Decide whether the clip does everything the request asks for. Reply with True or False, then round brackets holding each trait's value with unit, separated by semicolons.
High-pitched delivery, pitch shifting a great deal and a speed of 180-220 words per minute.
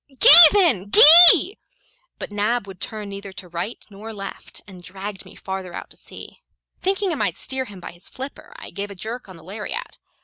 True (205 Hz; 6.3 semitones; 200 wpm)